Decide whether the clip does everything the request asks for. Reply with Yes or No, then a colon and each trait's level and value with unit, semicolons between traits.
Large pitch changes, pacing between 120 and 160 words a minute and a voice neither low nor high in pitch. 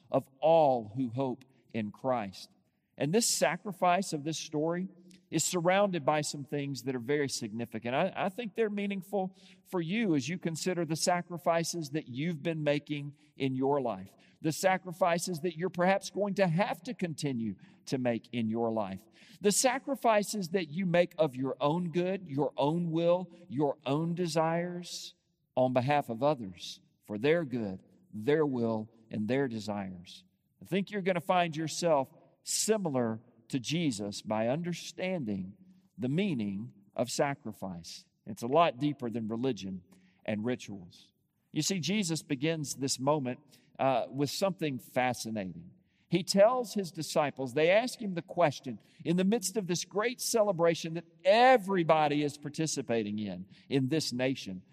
Yes: wide, 6.2 semitones; average, 155 wpm; medium, 155 Hz